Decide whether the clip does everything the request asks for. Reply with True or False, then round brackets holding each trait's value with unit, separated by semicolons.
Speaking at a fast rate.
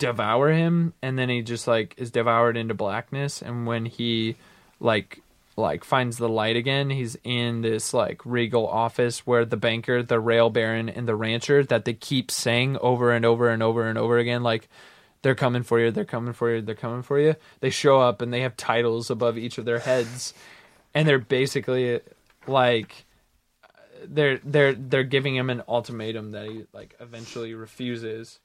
False (185 wpm)